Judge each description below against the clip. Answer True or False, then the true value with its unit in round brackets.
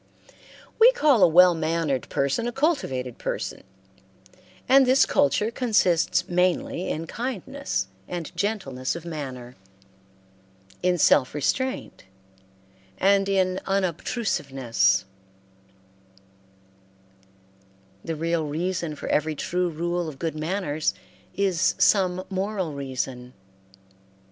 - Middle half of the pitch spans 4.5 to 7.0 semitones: True (4.8 semitones)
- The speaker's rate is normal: False (100 wpm)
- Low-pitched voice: False (175 Hz)